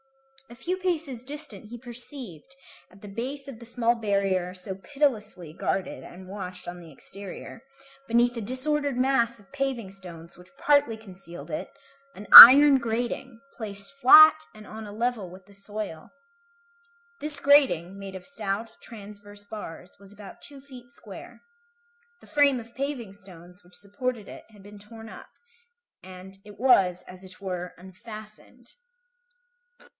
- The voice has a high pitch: Yes, high, 215 Hz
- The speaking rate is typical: Yes, average, 150 wpm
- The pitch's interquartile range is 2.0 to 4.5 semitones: No, average, 5.0 semitones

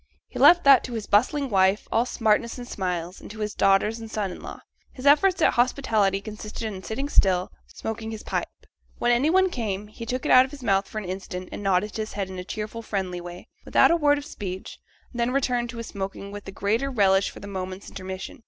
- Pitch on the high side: Yes, high, 215 Hz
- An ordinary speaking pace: No, fast, 235 wpm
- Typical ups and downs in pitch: Yes, average, 4.0 semitones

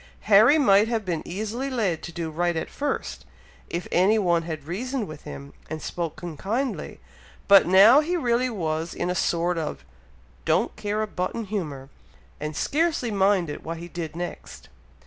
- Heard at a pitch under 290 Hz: Yes, medium, 185 Hz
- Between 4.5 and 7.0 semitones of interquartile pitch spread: Yes, average, 5.2 semitones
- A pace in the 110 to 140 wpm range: No, average, 165 wpm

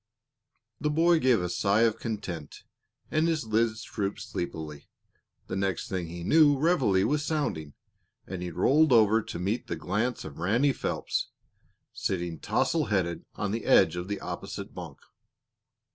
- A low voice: Yes, low, 105 Hz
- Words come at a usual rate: Yes, average, 155 wpm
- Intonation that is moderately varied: No, wide, 7.0 semitones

